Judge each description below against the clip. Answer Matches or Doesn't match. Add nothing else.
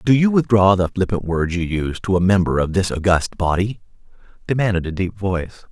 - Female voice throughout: Doesn't match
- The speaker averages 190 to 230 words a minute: Matches